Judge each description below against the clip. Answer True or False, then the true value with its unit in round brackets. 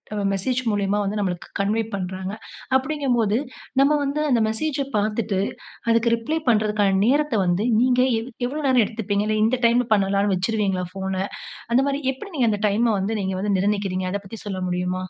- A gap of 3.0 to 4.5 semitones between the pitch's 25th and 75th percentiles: True (3.9 semitones)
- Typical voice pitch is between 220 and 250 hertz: False (210 Hz)